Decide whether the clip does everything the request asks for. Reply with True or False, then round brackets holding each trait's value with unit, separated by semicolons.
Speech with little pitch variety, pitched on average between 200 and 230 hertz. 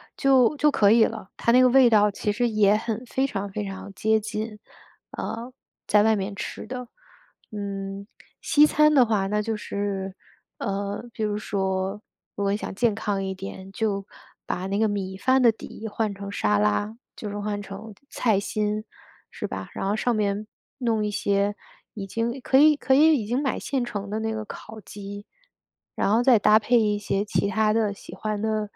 True (2.2 semitones; 210 Hz)